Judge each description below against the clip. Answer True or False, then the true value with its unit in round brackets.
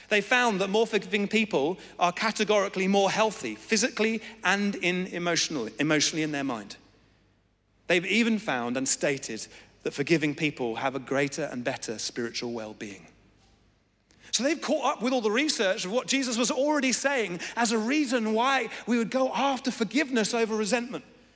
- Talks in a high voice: True (200 Hz)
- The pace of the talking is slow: False (165 wpm)